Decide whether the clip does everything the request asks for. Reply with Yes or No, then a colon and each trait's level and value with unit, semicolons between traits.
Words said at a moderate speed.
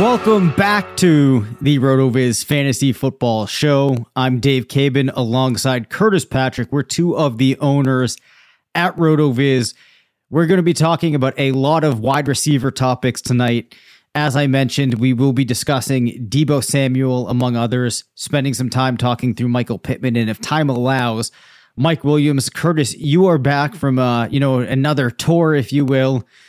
Yes: average, 160 wpm